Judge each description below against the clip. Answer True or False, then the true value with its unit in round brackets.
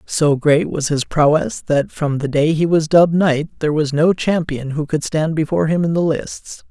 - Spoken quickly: True (225 wpm)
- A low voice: False (155 Hz)